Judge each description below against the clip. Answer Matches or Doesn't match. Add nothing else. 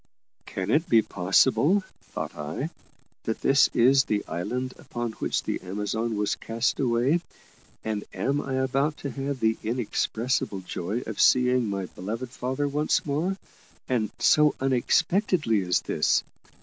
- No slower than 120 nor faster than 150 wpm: Matches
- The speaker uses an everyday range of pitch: Matches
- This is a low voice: Matches